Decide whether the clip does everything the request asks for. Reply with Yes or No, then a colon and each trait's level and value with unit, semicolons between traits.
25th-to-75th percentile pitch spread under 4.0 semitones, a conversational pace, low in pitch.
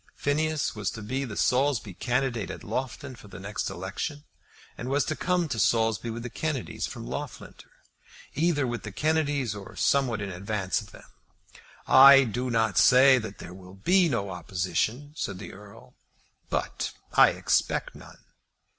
No: average, 5.3 semitones; average, 165 wpm; low, 120 Hz